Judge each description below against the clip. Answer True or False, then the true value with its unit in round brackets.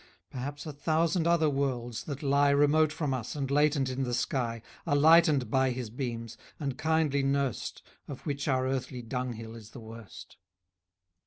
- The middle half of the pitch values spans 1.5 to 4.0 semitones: True (3.0 semitones)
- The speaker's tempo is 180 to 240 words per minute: False (165 wpm)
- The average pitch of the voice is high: False (135 Hz)